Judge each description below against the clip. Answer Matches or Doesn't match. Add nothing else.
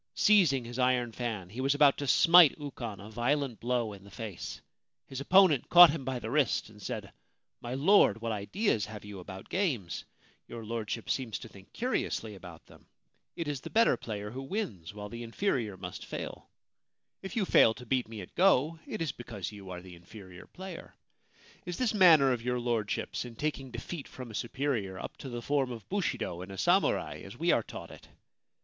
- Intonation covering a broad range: Matches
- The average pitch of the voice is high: Doesn't match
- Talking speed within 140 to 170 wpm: Doesn't match